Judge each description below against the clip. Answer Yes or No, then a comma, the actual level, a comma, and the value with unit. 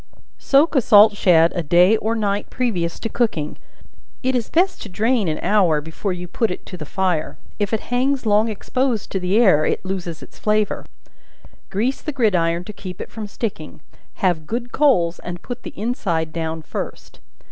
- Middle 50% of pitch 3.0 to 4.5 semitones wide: No, average, 5.0 semitones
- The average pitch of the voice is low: No, high, 205 Hz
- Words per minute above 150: Yes, average, 185 wpm